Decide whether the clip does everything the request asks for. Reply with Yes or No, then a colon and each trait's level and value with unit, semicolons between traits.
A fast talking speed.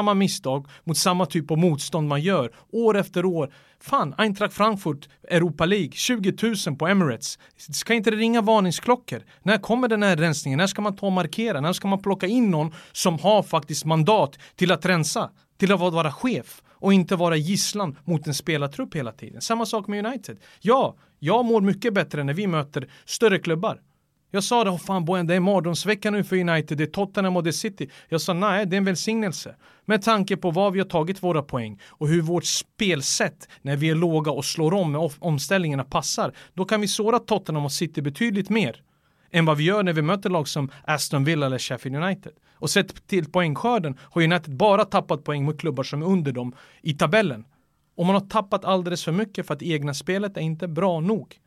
Yes: fast, 210 wpm